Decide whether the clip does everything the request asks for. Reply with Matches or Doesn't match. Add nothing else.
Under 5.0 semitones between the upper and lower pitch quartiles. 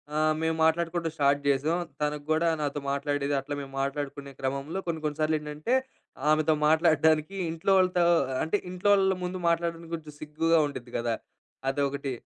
Matches